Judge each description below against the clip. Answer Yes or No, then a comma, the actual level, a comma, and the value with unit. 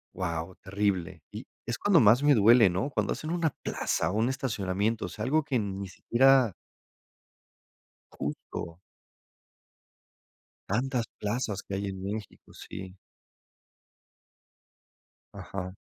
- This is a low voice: Yes, low, 105 Hz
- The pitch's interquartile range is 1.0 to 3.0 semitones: No, average, 5.0 semitones